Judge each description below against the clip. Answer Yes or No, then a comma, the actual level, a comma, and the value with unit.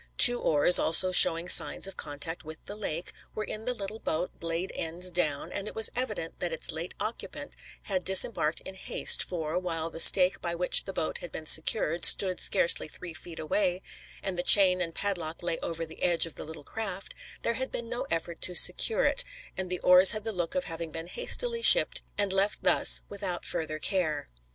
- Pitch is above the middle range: No, medium, 180 Hz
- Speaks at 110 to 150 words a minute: No, fast, 205 wpm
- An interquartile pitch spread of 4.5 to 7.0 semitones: No, average, 3.5 semitones